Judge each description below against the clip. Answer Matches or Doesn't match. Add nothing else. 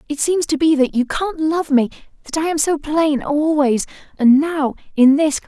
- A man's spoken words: Doesn't match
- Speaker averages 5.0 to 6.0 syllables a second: Doesn't match